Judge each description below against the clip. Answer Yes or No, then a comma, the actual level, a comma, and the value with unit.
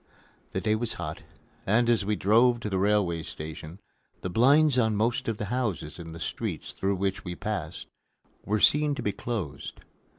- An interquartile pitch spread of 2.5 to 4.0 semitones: No, average, 4.6 semitones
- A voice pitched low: Yes, low, 105 Hz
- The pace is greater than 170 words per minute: Yes, average, 185 wpm